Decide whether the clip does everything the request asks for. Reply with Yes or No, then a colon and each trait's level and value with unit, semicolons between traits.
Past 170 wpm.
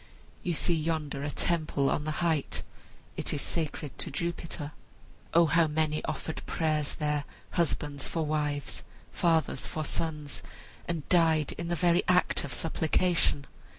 No: average, 145 wpm